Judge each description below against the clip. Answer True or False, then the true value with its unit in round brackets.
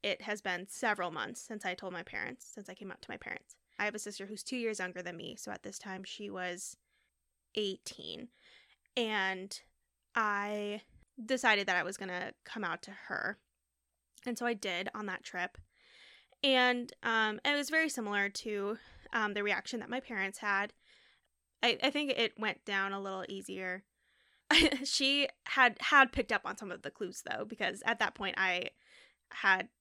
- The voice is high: True (210 Hz)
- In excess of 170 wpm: True (185 wpm)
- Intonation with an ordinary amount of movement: True (4.0 semitones)